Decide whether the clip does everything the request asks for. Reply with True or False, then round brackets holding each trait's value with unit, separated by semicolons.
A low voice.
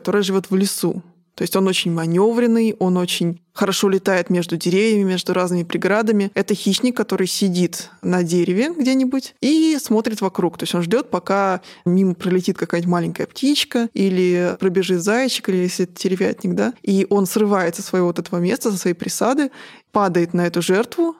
False (190 Hz)